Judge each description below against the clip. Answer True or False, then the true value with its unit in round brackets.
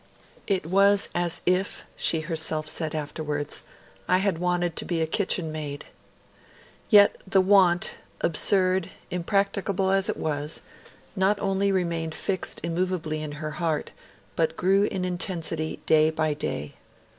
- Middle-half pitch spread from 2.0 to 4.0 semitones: True (3.3 semitones)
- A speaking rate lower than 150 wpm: True (140 wpm)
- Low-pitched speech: False (175 Hz)